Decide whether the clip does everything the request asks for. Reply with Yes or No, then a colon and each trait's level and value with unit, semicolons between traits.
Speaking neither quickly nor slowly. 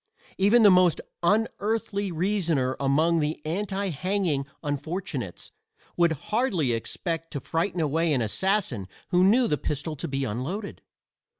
No: slow, 130 wpm